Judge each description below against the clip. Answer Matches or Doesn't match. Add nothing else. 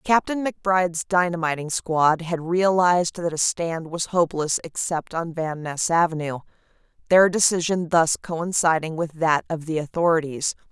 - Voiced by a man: Doesn't match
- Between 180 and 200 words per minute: Doesn't match